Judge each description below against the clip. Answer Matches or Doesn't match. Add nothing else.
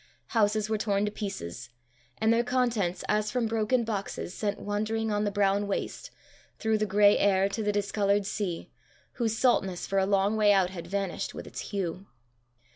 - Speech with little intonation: Matches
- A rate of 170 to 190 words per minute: Matches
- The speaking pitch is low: Doesn't match